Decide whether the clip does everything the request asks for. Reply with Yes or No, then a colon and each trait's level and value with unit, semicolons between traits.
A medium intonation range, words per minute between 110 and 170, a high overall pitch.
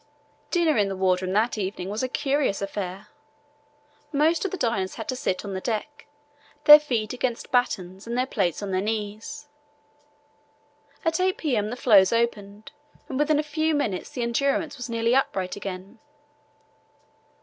No: wide, 5.9 semitones; average, 160 wpm; high, 230 Hz